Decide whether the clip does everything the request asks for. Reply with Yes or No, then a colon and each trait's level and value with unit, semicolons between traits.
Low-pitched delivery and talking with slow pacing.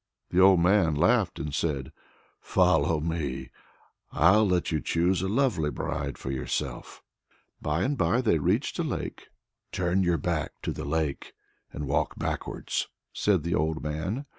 No: very low, 85 Hz; average, 160 wpm